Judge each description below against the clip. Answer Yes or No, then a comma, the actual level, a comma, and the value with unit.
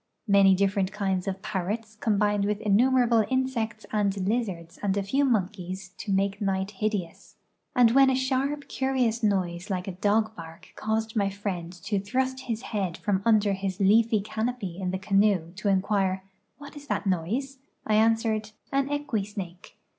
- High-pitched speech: Yes, high, 205 Hz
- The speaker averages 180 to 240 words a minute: No, average, 170 wpm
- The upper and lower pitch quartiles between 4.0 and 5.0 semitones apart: No, average, 3.0 semitones